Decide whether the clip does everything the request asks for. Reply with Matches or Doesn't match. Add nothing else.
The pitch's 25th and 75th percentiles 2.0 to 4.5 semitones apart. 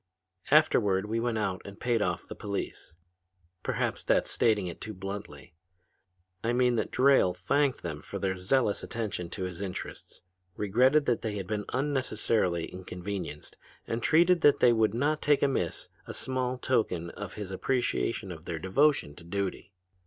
Doesn't match